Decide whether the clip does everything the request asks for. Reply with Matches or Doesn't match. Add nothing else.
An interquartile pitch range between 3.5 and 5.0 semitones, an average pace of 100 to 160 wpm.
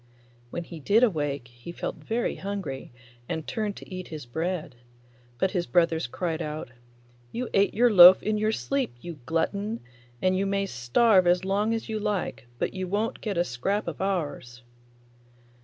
Doesn't match